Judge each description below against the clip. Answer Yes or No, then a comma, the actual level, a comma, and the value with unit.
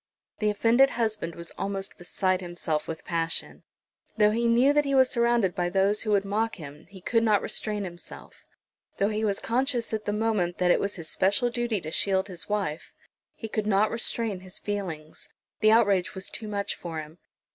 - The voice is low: No, high, 205 Hz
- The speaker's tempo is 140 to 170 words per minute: No, average, 195 wpm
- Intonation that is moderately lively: Yes, average, 4.0 semitones